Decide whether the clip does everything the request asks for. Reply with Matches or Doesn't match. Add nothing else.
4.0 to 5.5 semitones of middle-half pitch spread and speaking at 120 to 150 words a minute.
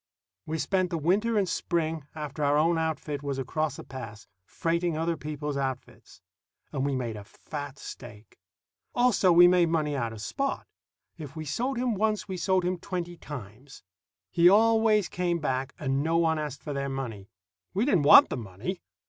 Doesn't match